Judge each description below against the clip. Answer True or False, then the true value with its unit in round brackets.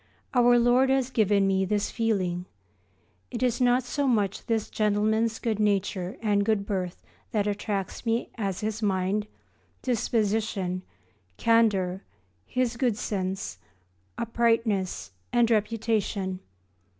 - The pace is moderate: False (115 wpm)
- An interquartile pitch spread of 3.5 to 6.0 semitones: False (2.9 semitones)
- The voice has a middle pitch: False (215 Hz)